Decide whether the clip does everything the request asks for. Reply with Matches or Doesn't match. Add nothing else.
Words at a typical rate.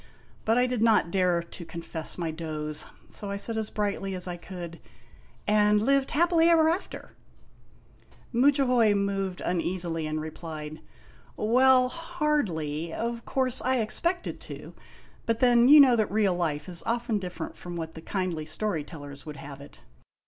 Matches